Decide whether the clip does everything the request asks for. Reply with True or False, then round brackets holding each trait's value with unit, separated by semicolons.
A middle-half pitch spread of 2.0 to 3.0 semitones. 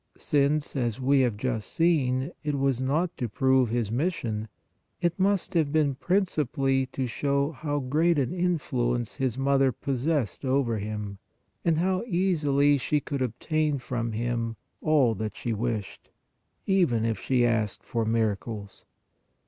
False (4.4 semitones)